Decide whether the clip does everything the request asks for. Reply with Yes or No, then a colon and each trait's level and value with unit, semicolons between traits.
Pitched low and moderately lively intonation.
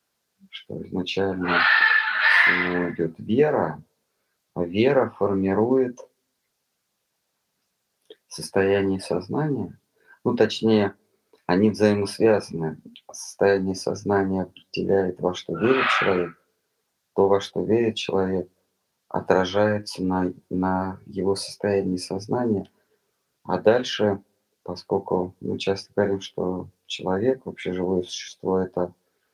No: very low, 95 Hz; narrow, 1.8 semitones